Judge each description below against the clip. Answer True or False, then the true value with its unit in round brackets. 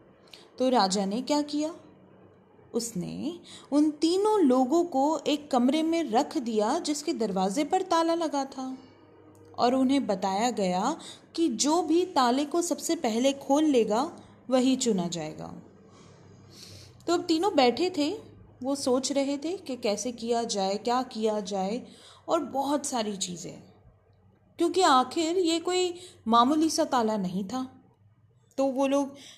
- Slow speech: False (140 wpm)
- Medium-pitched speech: False (270 Hz)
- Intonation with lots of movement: True (5.7 semitones)